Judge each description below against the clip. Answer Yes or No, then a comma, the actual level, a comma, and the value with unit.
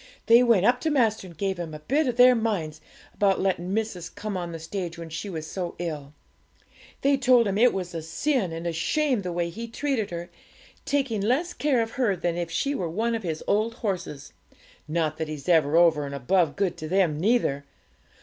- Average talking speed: No, fast, 210 wpm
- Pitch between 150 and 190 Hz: Yes, medium, 185 Hz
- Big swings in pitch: Yes, wide, 5.8 semitones